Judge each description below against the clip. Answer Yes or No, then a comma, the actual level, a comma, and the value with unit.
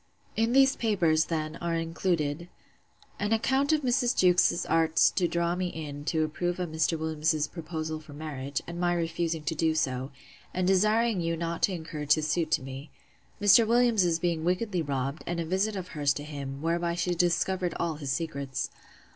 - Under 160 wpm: No, average, 180 wpm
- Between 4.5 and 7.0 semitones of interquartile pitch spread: No, average, 2.8 semitones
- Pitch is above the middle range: No, medium, 165 Hz